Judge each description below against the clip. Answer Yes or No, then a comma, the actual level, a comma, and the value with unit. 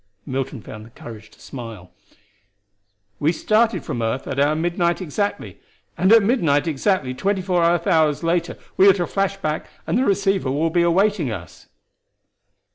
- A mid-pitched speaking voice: Yes, medium, 170 Hz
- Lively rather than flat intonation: Yes, wide, 6.2 semitones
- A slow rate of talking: No, average, 165 wpm